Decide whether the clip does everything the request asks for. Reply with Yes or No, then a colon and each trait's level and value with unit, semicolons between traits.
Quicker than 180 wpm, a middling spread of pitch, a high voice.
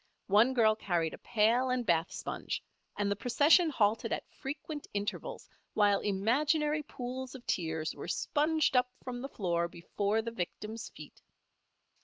No: average, 150 wpm; average, 4.7 semitones; high, 230 Hz